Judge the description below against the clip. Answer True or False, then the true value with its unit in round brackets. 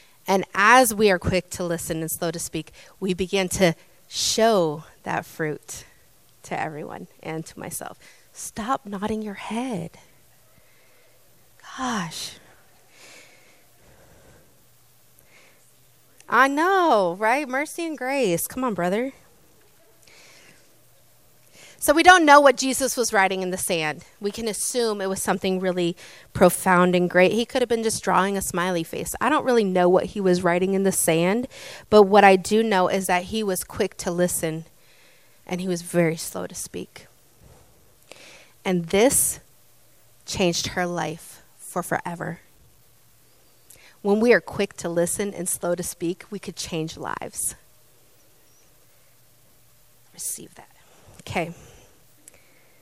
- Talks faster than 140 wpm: False (135 wpm)